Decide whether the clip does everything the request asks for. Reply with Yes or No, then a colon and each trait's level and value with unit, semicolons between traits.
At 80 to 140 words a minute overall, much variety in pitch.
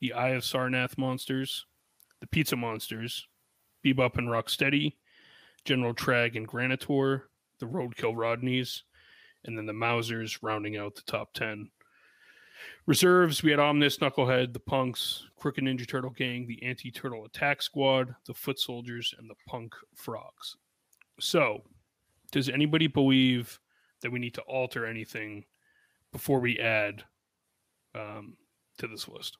No: slow, 135 wpm; average, 2.7 semitones